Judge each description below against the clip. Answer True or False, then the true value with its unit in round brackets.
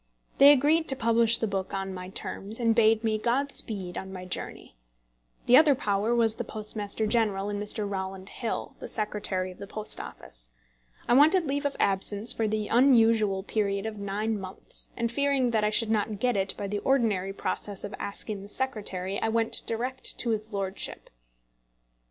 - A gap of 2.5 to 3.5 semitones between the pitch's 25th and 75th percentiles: True (3.0 semitones)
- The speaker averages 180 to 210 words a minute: True (185 wpm)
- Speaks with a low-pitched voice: False (215 Hz)